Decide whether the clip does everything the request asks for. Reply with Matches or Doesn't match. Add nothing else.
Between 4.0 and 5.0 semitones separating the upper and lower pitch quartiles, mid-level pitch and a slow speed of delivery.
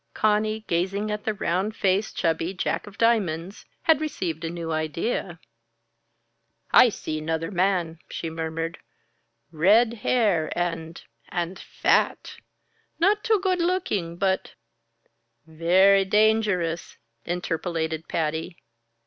Matches